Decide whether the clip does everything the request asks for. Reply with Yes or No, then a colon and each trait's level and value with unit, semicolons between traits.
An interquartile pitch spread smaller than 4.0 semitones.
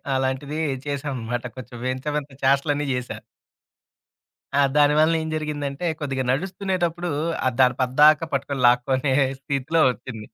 Yes: average, 2.7 semitones